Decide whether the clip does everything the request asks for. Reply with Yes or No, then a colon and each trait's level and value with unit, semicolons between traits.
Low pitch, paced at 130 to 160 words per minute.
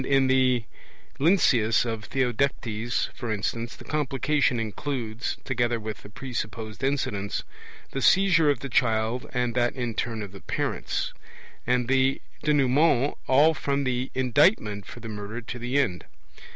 Yes: low, 125 Hz; average, 145 wpm